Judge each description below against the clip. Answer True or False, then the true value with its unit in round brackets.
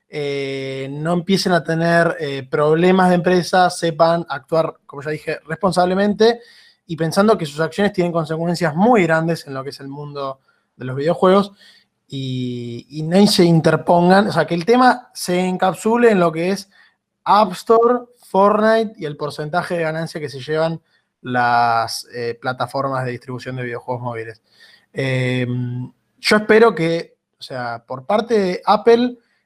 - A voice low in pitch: False (165 Hz)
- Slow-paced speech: False (160 wpm)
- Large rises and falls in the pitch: True (5.8 semitones)